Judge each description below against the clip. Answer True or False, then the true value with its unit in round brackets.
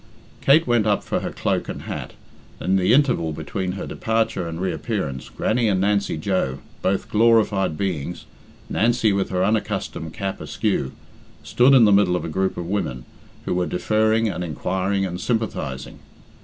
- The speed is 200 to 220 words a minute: False (170 wpm)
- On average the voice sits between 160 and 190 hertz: False (95 Hz)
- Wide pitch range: False (3.7 semitones)